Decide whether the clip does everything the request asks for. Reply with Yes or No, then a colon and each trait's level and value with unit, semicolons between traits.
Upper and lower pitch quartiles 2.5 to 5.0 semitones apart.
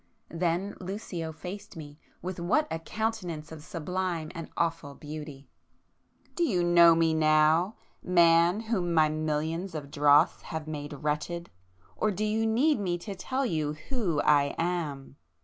Yes: average, 3.3 semitones